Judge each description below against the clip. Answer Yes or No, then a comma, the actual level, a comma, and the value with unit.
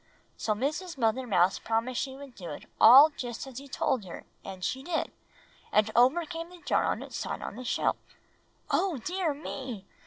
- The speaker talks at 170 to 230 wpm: Yes, average, 190 wpm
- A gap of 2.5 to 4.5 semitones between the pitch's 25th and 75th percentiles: No, average, 5.3 semitones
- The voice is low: No, very high, 260 Hz